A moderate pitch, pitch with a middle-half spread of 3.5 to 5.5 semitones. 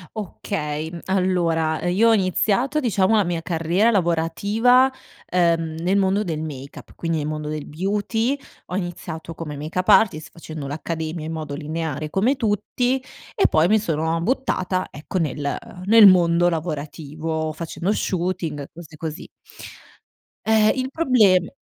Yes: medium, 170 Hz; average, 4.2 semitones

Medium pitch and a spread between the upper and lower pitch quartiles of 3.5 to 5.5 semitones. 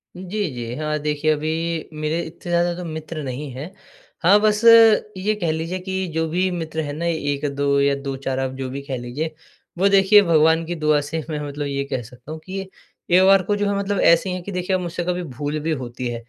Yes: medium, 160 Hz; average, 4.2 semitones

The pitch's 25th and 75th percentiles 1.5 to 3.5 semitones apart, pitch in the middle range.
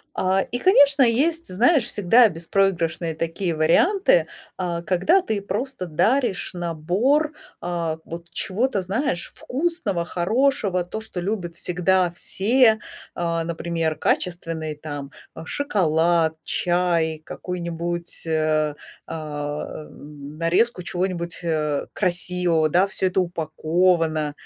No: average, 4.2 semitones; medium, 175 Hz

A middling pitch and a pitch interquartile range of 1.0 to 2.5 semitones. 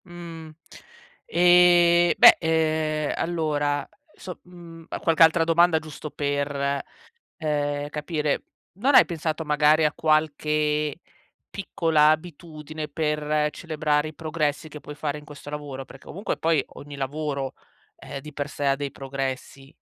Yes: medium, 150 Hz; narrow, 2.0 semitones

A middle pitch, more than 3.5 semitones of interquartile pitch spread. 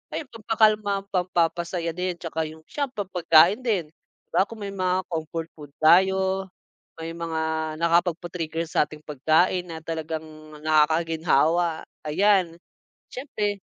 No: medium, 170 Hz; average, 3.1 semitones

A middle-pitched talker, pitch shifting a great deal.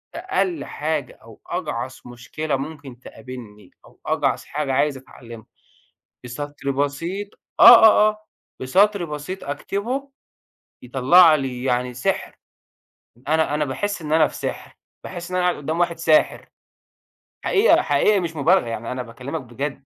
Yes: medium, 150 Hz; wide, 5.7 semitones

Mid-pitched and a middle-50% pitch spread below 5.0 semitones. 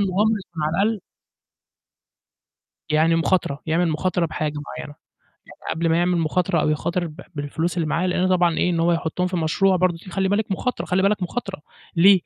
Yes: medium, 175 Hz; narrow, 2.5 semitones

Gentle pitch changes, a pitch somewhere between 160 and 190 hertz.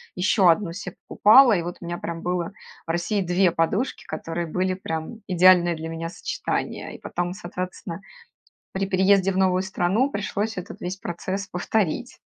Yes: narrow, 2.3 semitones; medium, 185 Hz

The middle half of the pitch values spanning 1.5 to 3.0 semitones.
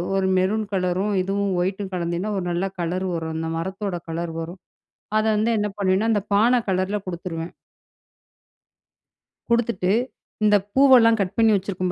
Yes: average, 2.7 semitones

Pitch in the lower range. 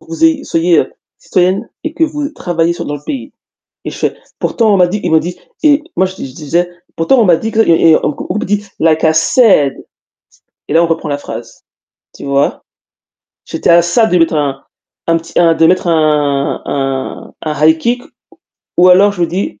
No: medium, 170 Hz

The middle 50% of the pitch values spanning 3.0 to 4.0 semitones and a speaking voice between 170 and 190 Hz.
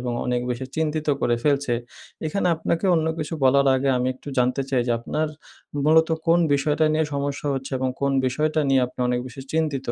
No: average, 3.3 semitones; medium, 140 Hz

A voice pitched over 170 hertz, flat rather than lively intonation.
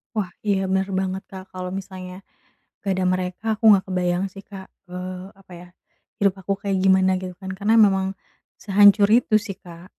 Yes: high, 190 Hz; narrow, 1.3 semitones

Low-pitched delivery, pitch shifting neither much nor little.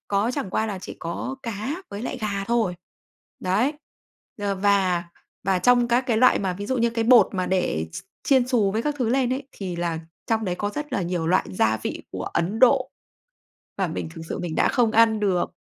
No: high, 210 Hz; average, 4.9 semitones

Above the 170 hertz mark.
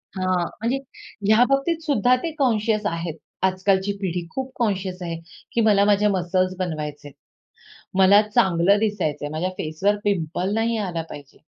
Yes: high, 190 Hz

